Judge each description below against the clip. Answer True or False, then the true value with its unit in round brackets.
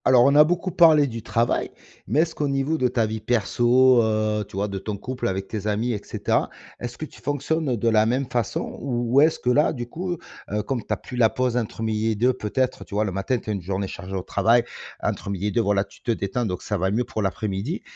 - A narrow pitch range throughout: False (3.8 semitones)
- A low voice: True (115 Hz)